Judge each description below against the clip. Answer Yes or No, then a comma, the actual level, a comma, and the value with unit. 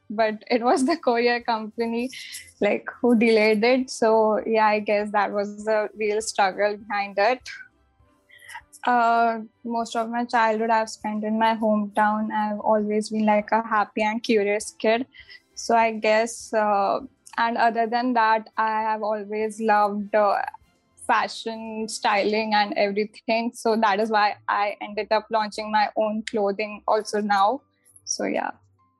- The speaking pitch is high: Yes, high, 220 Hz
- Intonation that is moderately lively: No, narrow, 1.7 semitones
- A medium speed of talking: Yes, average, 150 wpm